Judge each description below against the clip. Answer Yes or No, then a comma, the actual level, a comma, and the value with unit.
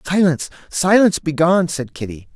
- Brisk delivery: No, slow, 125 wpm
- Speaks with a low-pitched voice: No, medium, 160 Hz